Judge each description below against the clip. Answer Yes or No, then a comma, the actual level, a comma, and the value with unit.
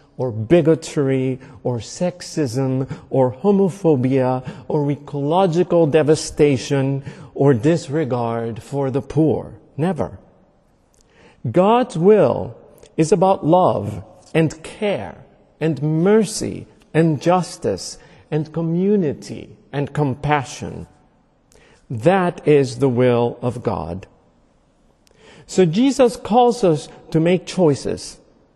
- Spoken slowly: Yes, slow, 90 wpm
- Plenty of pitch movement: No, average, 5.0 semitones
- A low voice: No, medium, 150 Hz